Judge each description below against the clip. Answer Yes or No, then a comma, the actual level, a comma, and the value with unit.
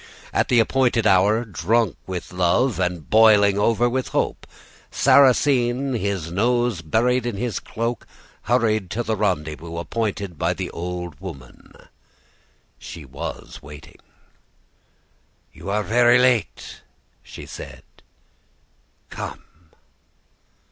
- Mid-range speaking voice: No, low, 105 Hz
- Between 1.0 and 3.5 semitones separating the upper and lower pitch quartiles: No, average, 5.1 semitones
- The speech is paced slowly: Yes, slow, 110 wpm